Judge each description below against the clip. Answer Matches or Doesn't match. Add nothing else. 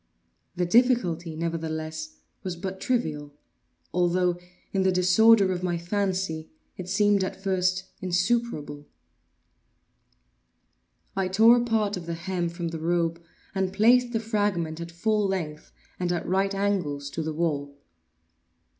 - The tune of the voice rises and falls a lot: Doesn't match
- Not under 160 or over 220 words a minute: Doesn't match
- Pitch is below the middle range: Doesn't match